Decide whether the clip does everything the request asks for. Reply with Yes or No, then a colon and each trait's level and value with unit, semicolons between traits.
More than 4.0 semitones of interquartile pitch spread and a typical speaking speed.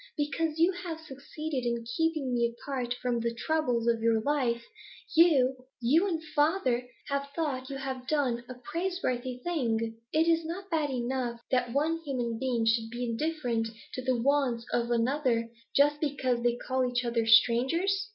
Yes: average, 4.4 semitones; average, 165 wpm